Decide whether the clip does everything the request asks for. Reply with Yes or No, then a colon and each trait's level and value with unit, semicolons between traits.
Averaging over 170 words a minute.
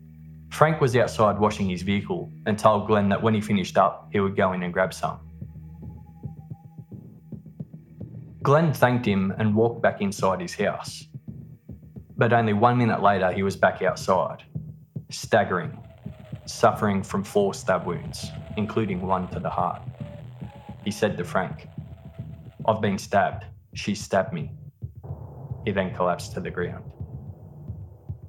No: average, 140 wpm